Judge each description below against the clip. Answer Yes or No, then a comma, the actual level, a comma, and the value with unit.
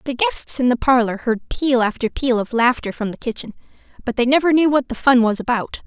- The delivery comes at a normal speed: No, fast, 235 wpm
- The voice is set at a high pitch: Yes, very high, 250 Hz